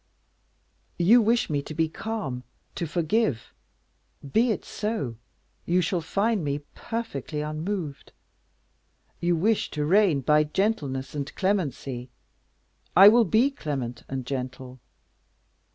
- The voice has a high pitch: No, medium, 160 Hz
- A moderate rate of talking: No, slow, 120 wpm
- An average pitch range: No, wide, 7.1 semitones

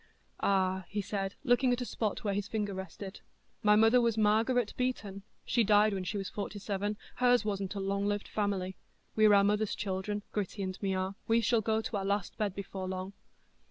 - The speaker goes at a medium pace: Yes, average, 195 wpm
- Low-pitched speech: No, high, 205 Hz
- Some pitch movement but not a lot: No, narrow, 2.0 semitones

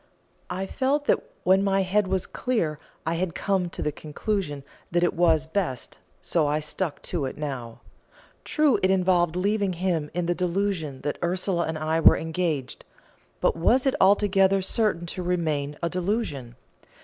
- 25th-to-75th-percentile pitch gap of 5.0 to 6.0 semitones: No, average, 3.6 semitones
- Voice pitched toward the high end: No, medium, 175 Hz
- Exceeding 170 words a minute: No, average, 165 wpm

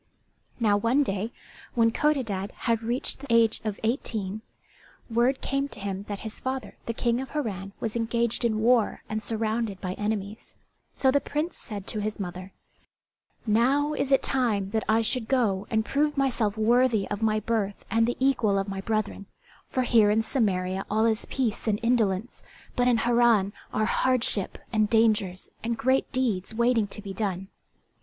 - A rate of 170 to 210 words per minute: Yes, average, 175 wpm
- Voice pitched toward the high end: Yes, high, 225 Hz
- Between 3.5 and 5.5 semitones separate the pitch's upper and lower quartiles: No, average, 3.0 semitones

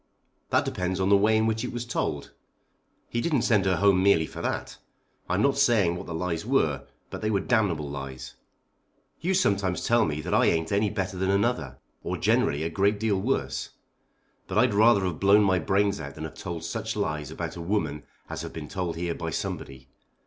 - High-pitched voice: No, very low, 95 Hz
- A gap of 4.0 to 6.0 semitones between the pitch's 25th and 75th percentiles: Yes, average, 4.6 semitones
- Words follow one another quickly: Yes, fast, 210 wpm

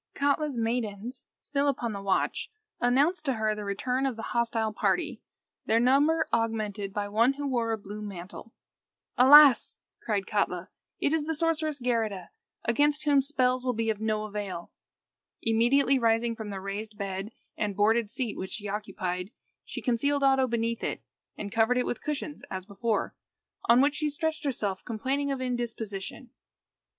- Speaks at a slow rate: No, average, 160 wpm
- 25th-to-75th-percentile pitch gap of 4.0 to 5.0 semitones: Yes, average, 4.6 semitones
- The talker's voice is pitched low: No, high, 230 Hz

